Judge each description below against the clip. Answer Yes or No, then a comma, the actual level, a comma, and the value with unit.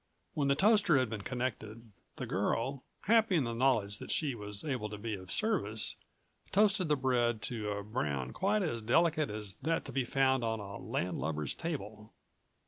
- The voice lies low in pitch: Yes, low, 120 Hz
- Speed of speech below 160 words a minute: No, average, 180 wpm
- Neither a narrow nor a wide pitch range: No, wide, 6.2 semitones